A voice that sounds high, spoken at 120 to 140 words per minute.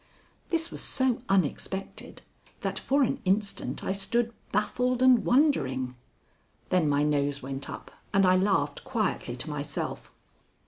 Yes: high, 195 Hz; slow, 135 wpm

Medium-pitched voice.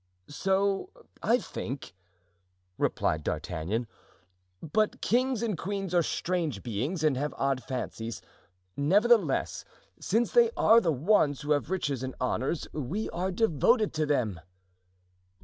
Yes: medium, 160 Hz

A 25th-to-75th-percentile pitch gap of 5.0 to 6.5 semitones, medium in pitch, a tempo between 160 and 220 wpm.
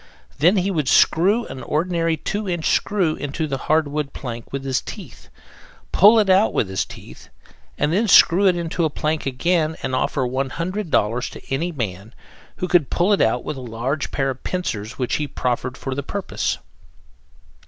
Yes: wide, 5.4 semitones; medium, 150 Hz; average, 180 wpm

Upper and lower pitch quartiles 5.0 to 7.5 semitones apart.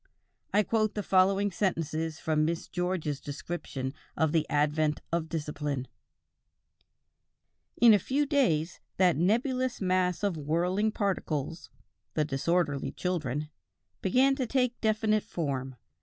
Yes: wide, 5.4 semitones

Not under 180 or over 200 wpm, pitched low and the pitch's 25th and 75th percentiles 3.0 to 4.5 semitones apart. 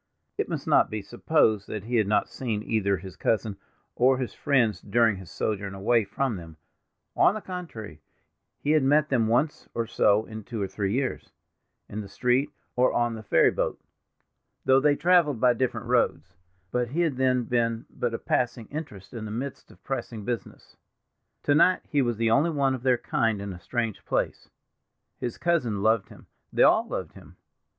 Yes: average, 185 wpm; low, 115 Hz; average, 4.0 semitones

